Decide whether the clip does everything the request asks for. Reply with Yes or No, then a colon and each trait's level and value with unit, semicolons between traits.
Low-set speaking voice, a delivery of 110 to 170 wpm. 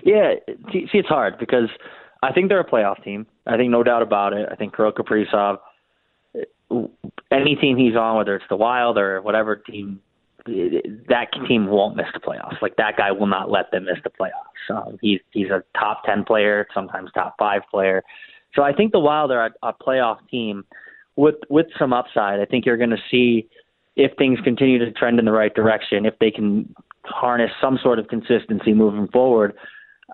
No: low, 120 Hz; average, 195 wpm